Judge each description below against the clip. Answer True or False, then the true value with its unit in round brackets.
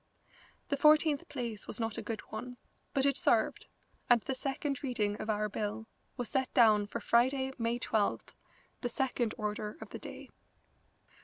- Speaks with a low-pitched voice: False (235 Hz)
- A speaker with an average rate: True (165 wpm)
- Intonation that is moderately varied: True (3.7 semitones)